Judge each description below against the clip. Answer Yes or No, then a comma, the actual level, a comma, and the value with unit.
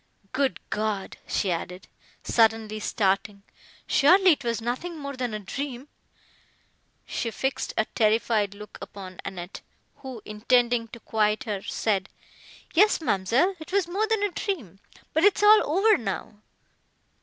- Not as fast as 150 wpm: Yes, average, 140 wpm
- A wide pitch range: Yes, wide, 6.7 semitones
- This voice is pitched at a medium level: No, high, 230 Hz